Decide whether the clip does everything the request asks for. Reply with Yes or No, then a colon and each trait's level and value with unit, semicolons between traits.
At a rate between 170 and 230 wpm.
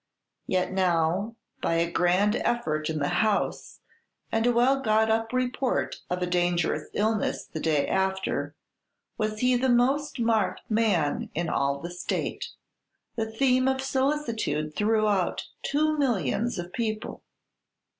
No: slow, 135 wpm